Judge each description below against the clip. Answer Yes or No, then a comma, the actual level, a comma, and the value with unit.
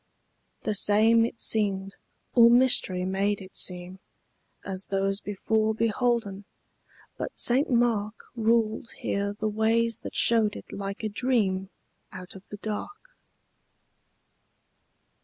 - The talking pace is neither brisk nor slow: No, slow, 120 wpm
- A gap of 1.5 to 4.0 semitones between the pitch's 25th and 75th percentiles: Yes, average, 2.8 semitones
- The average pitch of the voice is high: Yes, high, 210 Hz